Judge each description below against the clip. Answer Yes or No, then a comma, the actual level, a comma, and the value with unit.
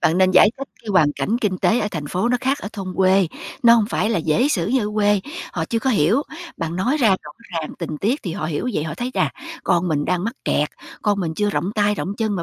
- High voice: Yes, high, 200 Hz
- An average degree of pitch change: Yes, average, 4.7 semitones